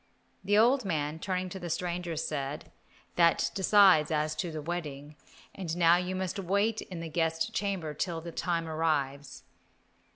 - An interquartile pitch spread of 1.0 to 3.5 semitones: Yes, average, 3.2 semitones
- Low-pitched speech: No, medium, 170 Hz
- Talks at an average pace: Yes, average, 160 wpm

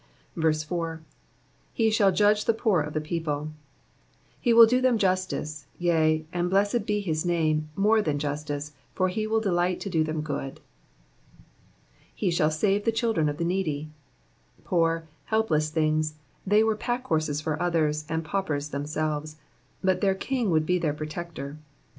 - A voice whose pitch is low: No, medium, 165 Hz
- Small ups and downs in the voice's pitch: No, average, 4.5 semitones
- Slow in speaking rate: No, average, 155 wpm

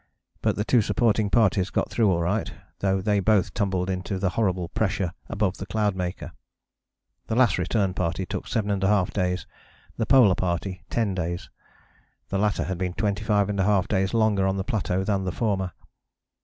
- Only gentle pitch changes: Yes, narrow, 2.2 semitones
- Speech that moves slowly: No, average, 165 wpm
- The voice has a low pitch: Yes, very low, 95 Hz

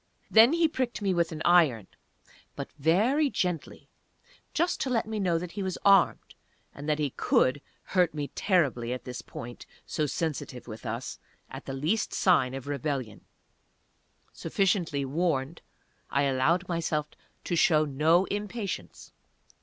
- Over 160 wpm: No, average, 145 wpm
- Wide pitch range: Yes, wide, 5.8 semitones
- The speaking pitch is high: No, medium, 165 Hz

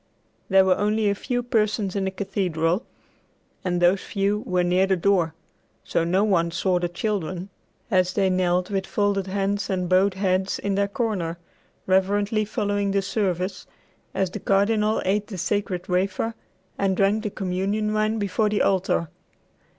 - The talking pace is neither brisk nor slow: Yes, average, 160 wpm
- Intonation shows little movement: Yes, narrow, 2.0 semitones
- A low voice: No, high, 195 Hz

